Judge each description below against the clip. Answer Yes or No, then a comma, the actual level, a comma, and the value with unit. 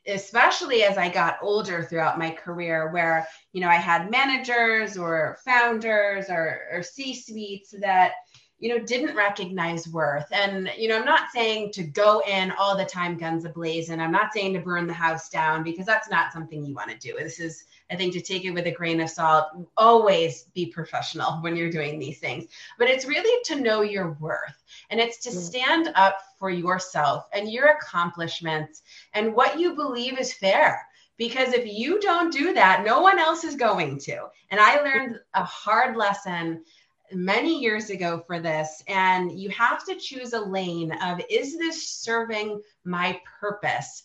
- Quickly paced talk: No, average, 185 wpm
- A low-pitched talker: No, high, 195 Hz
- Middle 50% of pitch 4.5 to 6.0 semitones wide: Yes, wide, 5.5 semitones